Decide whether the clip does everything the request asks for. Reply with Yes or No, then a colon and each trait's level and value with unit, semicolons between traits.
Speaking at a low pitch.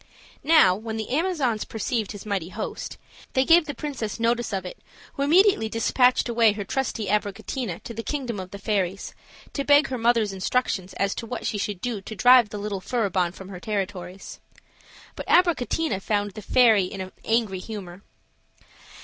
No: high, 220 Hz